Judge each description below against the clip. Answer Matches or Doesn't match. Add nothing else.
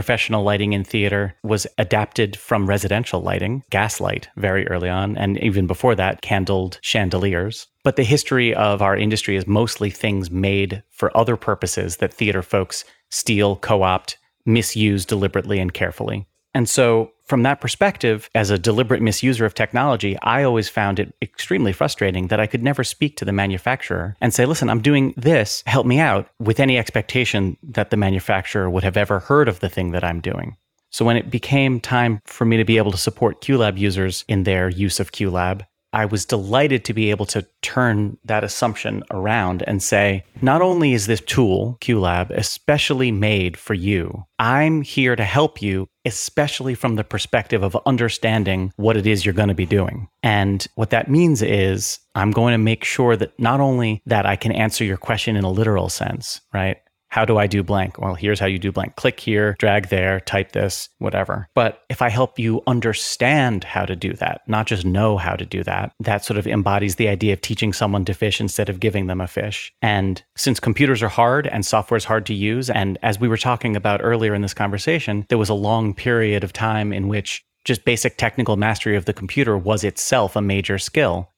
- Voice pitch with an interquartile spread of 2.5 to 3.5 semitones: Matches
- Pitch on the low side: Matches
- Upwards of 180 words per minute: Matches